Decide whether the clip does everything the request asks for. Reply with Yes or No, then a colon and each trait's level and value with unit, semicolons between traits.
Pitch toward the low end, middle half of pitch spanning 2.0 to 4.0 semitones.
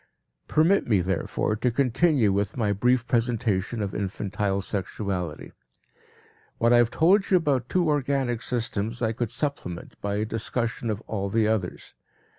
Yes: low, 115 Hz; average, 3.7 semitones